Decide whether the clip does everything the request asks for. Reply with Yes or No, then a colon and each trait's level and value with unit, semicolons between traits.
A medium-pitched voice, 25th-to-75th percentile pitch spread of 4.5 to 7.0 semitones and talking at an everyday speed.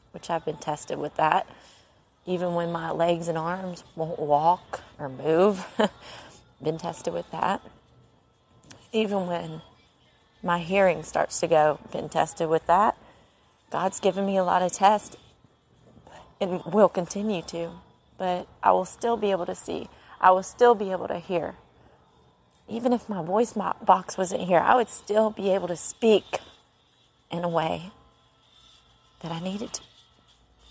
No: medium, 180 Hz; average, 3.3 semitones; average, 150 wpm